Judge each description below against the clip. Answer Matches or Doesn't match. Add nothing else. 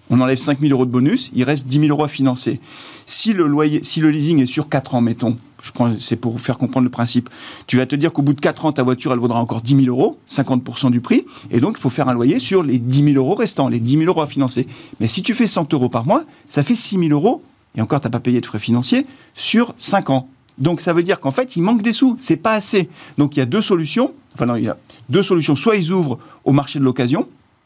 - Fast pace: Matches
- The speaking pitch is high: Doesn't match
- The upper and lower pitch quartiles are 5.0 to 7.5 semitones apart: Matches